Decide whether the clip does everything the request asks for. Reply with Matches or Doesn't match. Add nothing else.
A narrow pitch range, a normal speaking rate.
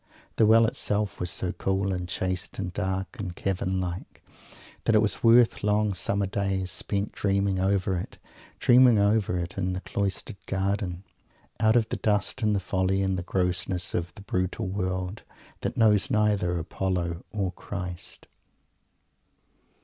Matches